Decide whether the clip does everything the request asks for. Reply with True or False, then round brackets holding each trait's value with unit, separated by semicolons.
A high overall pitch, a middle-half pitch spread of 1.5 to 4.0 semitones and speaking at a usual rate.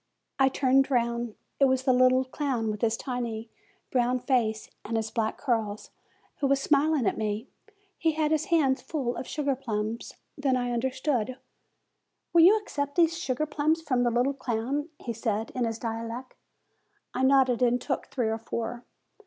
True (255 Hz; 3.2 semitones; 170 wpm)